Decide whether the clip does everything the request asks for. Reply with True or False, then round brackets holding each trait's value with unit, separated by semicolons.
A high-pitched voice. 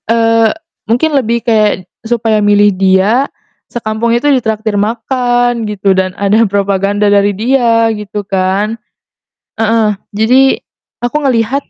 True (220 Hz)